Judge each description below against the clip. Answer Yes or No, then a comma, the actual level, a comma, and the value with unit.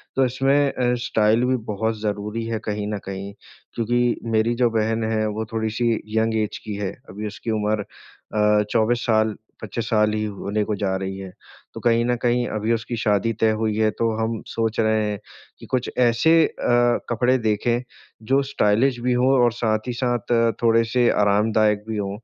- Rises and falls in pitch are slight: Yes, narrow, 2.1 semitones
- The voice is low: Yes, low, 110 Hz